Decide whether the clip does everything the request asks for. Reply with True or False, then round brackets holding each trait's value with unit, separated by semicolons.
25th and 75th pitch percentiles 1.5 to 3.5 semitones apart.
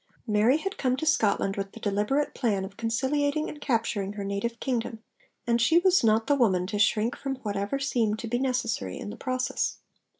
False (4.5 semitones)